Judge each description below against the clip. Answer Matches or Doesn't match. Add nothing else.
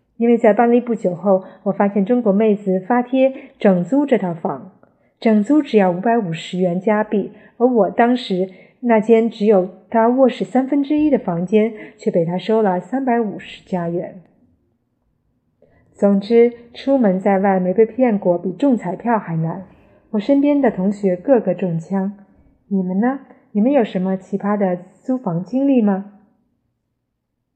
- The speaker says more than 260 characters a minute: Doesn't match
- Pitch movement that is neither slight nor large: Matches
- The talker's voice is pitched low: Doesn't match